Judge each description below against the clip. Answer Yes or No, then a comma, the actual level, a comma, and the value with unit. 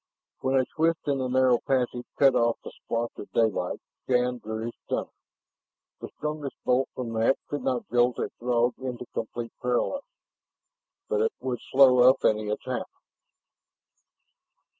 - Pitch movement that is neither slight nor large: No, narrow, 2.1 semitones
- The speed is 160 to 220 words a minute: No, average, 150 wpm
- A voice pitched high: No, low, 125 Hz